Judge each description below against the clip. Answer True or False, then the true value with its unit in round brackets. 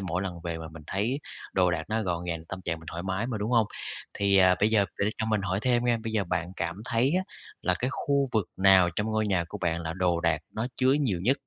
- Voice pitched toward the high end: False (95 Hz)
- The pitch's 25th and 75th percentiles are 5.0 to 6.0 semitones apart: False (4.2 semitones)